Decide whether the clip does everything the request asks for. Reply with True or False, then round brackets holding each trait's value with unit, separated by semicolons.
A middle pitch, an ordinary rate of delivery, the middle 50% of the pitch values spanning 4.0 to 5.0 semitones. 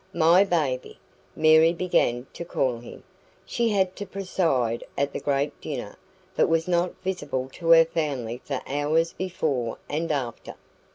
True (155 Hz; 150 wpm; 4.6 semitones)